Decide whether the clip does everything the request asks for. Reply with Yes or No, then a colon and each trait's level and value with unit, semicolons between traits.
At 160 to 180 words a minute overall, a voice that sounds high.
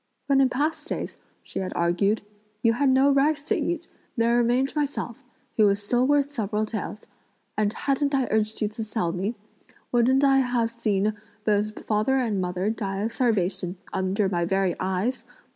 Yes: average, 175 wpm; high, 225 Hz